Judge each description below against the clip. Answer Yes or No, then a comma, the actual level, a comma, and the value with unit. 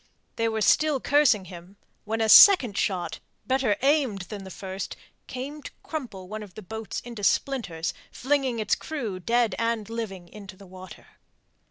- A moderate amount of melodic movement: Yes, average, 5.0 semitones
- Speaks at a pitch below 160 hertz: No, high, 220 Hz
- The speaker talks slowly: No, average, 165 wpm